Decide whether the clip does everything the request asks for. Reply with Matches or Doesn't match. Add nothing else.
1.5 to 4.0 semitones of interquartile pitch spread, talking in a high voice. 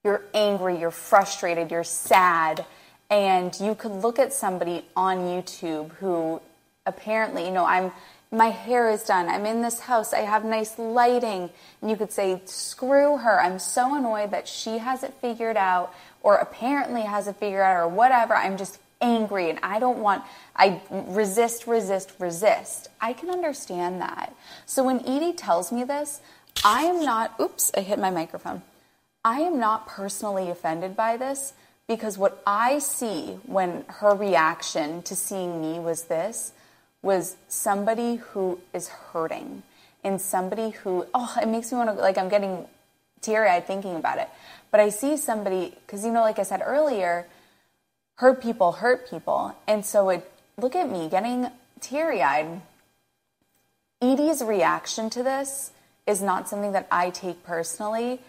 Doesn't match